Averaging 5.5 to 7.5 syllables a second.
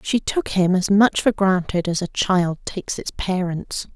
No: 4.3 syllables/s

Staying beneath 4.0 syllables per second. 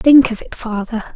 No: 4.9 syllables/s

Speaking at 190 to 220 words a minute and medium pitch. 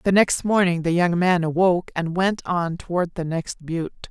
Yes: fast, 205 wpm; medium, 175 Hz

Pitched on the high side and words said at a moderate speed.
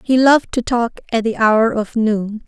No: high, 230 Hz; fast, 220 wpm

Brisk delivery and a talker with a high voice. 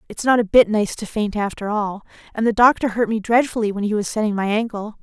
Yes: fast, 250 wpm; high, 215 Hz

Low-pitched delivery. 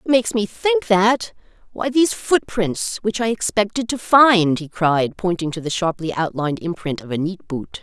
No: high, 190 Hz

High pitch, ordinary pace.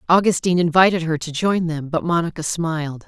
No: medium, 165 Hz; average, 175 wpm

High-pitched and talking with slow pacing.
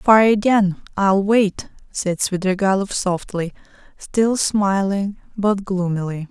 Yes: high, 195 Hz; slow, 105 wpm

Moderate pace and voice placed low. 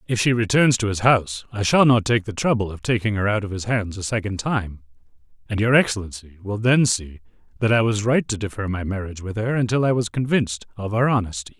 No: fast, 235 wpm; low, 105 Hz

